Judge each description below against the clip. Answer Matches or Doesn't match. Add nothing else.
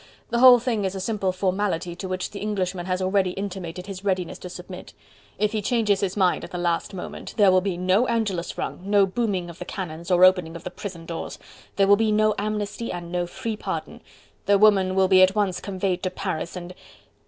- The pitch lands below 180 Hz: Doesn't match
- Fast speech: Matches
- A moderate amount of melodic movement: Doesn't match